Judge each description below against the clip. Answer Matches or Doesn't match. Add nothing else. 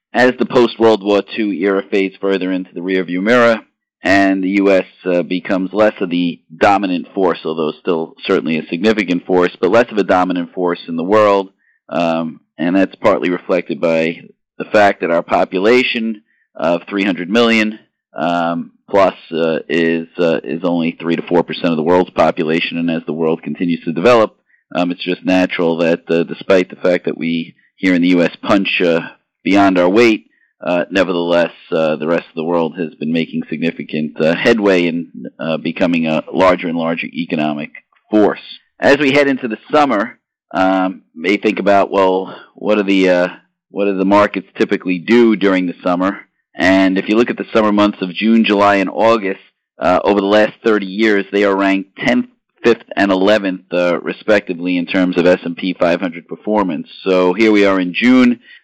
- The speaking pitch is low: Matches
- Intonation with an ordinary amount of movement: Matches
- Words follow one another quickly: Doesn't match